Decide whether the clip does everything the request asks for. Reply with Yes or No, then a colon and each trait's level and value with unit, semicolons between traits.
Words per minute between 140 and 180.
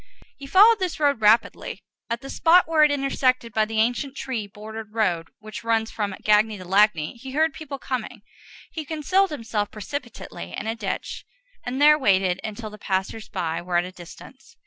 No: average, 190 wpm